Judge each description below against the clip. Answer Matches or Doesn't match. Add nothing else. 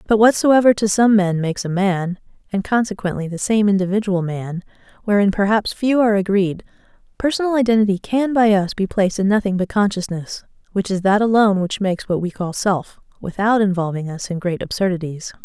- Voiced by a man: Doesn't match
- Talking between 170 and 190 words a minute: Matches